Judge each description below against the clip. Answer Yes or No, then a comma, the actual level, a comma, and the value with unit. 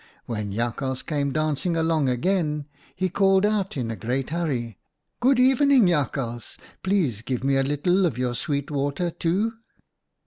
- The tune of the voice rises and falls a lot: Yes, wide, 6.4 semitones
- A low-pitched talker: No, medium, 150 Hz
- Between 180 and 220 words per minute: No, average, 160 wpm